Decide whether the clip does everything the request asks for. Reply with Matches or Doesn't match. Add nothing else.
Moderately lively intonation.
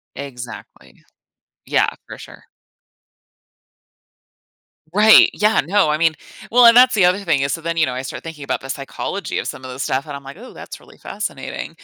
Doesn't match